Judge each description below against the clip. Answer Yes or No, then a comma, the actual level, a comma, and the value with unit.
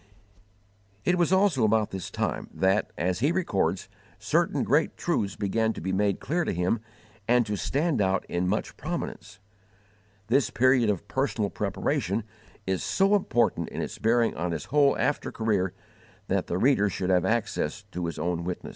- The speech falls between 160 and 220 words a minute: Yes, average, 170 wpm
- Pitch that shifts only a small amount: No, wide, 5.6 semitones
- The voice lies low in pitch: Yes, low, 105 Hz